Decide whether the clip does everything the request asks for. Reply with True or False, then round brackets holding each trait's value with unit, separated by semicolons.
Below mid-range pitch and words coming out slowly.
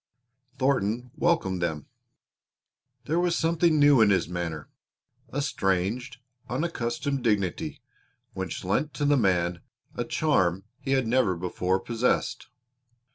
True (115 Hz; 120 wpm)